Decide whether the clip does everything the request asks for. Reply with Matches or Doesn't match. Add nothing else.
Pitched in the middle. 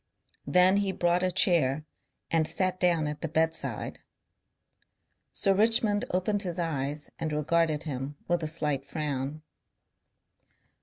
Matches